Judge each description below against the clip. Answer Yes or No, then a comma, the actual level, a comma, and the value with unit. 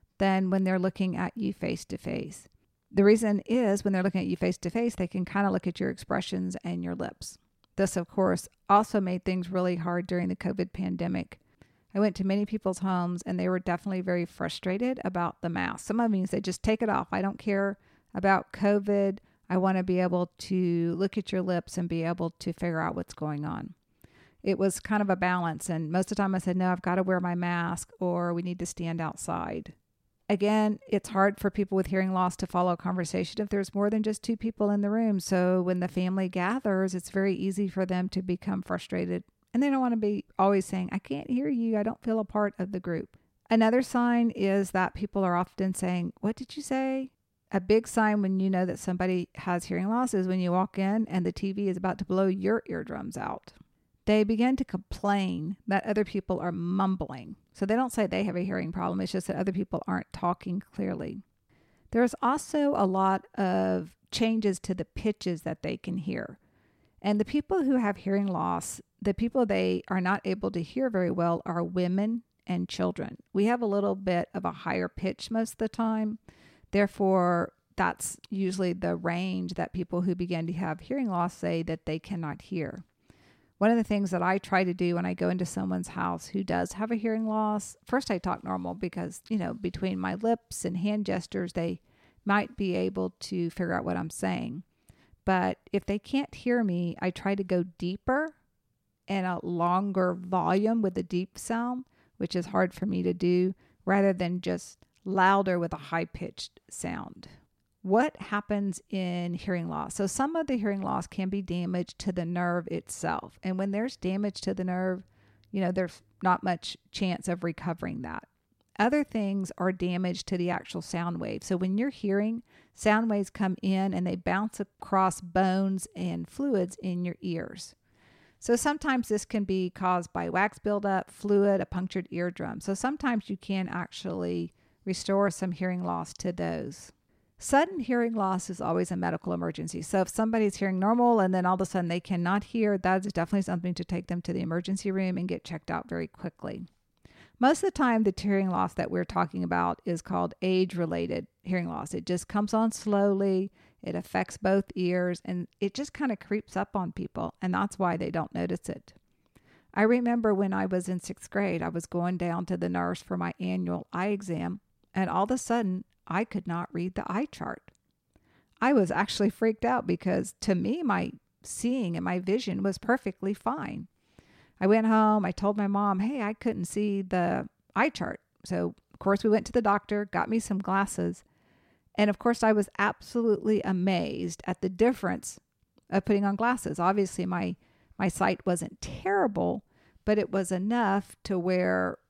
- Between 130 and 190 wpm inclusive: No, average, 200 wpm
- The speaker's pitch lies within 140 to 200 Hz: Yes, high, 190 Hz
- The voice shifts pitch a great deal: No, average, 2.8 semitones